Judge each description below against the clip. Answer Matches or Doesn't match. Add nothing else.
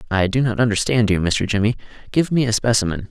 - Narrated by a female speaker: Doesn't match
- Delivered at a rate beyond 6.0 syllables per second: Matches